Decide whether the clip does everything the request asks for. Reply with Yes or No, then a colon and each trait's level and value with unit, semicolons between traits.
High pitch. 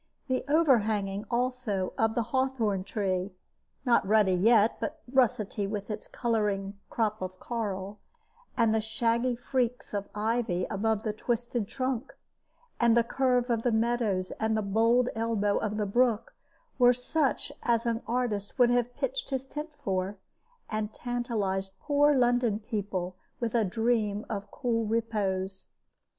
Yes: high, 225 Hz